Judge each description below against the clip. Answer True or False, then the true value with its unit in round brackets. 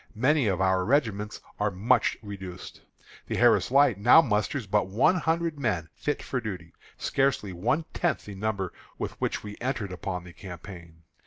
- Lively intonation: True (5.9 semitones)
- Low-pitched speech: True (105 Hz)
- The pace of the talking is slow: False (165 wpm)